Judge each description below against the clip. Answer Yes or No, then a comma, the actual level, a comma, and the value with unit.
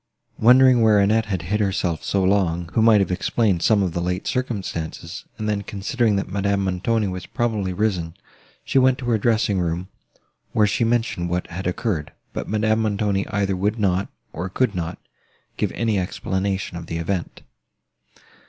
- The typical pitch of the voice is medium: No, low, 100 Hz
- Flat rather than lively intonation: No, average, 3.3 semitones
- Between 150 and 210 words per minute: Yes, average, 170 wpm